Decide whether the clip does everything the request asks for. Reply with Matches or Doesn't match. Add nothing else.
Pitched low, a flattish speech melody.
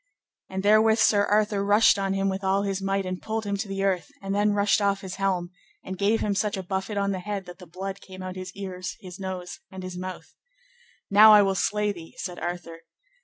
Doesn't match